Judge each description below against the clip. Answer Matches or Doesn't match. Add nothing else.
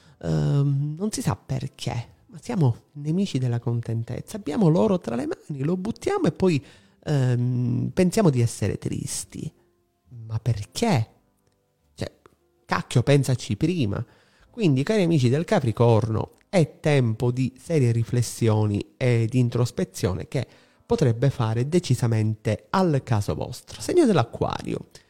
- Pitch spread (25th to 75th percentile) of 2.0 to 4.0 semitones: Doesn't match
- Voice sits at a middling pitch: Doesn't match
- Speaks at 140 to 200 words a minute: Doesn't match